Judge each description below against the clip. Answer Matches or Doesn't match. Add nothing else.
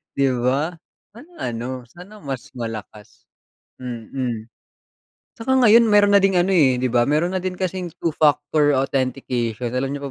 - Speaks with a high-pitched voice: Doesn't match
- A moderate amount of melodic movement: Doesn't match